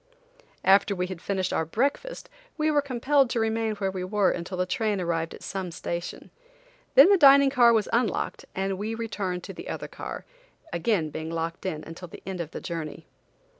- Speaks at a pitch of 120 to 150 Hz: No, high, 195 Hz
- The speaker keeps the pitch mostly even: No, average, 5.1 semitones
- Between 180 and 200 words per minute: Yes, average, 195 wpm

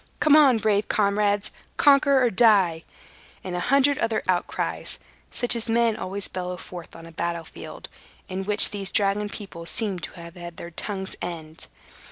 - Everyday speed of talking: Yes, average, 170 wpm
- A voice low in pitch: No, high, 200 Hz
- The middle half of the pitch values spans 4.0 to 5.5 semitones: Yes, average, 4.3 semitones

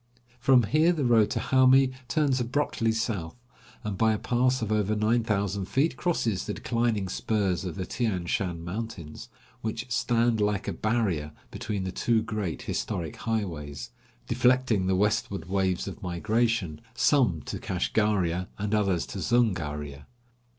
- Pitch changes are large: No, average, 4.3 semitones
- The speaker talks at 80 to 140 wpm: No, average, 150 wpm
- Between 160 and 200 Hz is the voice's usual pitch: No, low, 105 Hz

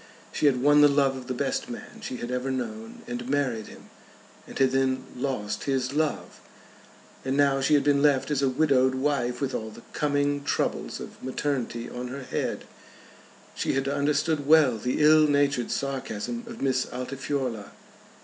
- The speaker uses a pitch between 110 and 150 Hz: Yes, low, 135 Hz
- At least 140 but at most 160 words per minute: No, average, 175 wpm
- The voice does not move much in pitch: Yes, narrow, 2.3 semitones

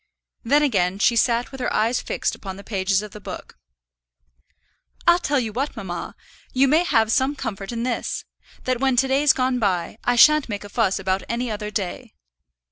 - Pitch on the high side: Yes, high, 235 Hz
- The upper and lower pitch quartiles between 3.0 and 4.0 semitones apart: No, average, 4.5 semitones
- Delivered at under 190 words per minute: No, average, 195 wpm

